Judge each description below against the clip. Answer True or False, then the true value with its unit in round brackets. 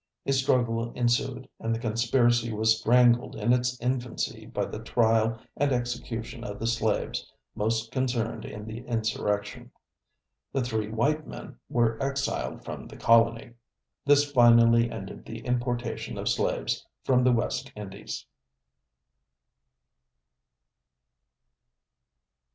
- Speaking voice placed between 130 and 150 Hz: False (120 Hz)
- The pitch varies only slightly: True (1.8 semitones)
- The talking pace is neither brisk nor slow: False (115 wpm)